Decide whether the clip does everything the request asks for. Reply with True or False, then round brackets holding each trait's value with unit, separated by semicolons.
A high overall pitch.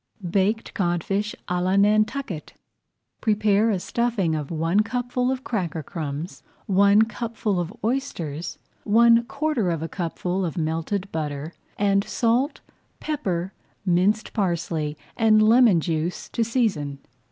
True (200 Hz)